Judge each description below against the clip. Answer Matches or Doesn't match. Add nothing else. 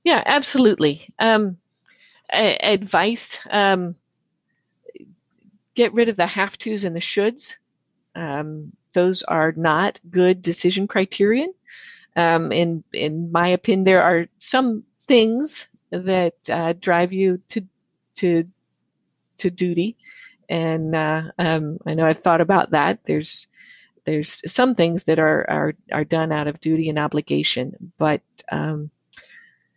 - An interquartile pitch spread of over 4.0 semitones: Matches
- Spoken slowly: Matches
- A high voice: Doesn't match